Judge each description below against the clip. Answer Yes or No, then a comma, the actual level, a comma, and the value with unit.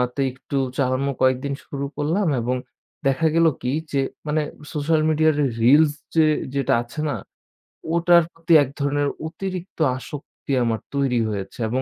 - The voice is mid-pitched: Yes, medium, 145 Hz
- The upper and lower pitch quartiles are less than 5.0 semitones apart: Yes, average, 3.5 semitones